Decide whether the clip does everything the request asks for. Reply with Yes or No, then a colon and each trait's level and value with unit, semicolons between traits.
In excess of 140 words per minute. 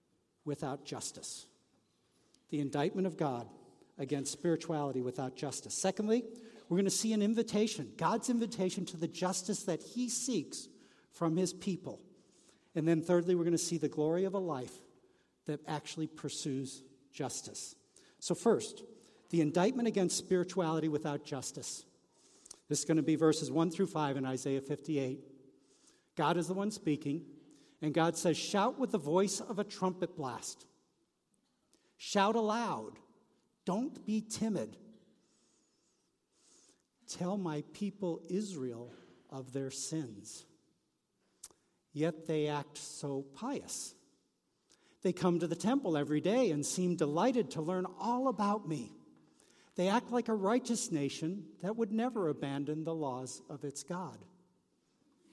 No: slow, 135 wpm